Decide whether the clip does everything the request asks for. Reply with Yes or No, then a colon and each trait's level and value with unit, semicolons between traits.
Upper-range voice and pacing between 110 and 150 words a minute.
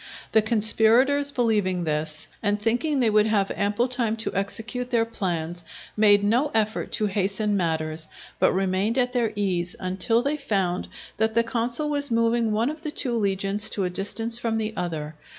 No: high, 215 Hz; average, 175 wpm